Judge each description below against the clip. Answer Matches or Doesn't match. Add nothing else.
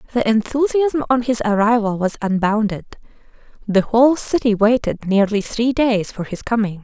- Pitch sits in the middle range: Doesn't match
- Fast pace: Doesn't match